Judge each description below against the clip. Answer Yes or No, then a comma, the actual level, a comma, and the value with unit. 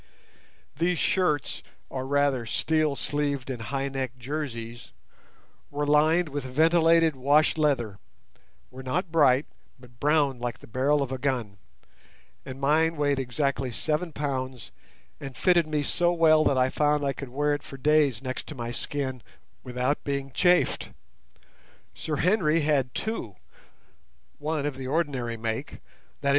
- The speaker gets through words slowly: No, average, 145 wpm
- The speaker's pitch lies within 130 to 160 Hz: Yes, medium, 140 Hz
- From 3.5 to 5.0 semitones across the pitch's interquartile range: No, average, 3.0 semitones